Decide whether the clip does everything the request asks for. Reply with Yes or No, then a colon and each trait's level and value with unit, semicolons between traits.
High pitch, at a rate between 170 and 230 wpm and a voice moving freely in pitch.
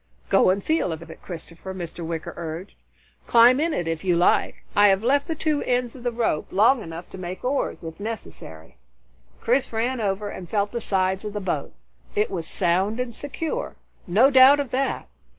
Yes: high, 205 Hz; average, 195 wpm; wide, 6.2 semitones